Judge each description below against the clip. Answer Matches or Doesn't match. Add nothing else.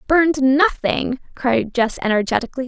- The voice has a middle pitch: Doesn't match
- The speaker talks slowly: Matches